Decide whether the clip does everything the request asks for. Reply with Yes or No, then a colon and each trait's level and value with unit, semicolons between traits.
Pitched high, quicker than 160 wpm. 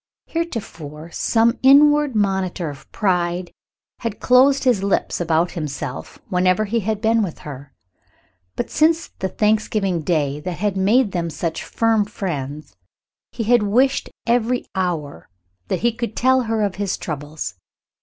No: high, 195 Hz; average, 145 wpm